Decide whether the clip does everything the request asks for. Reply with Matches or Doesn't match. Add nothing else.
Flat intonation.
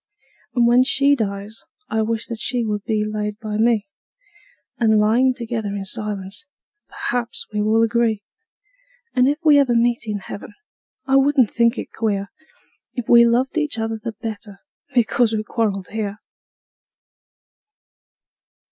Matches